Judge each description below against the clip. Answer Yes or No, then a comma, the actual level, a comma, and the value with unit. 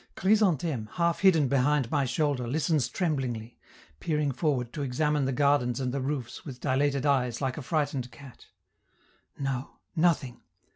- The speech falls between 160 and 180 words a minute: No, average, 145 wpm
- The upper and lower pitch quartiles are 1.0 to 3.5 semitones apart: Yes, average, 3.1 semitones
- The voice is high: No, medium, 140 Hz